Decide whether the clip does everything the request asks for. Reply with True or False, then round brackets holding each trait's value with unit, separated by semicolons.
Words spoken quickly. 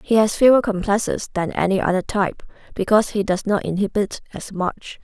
False (180 wpm)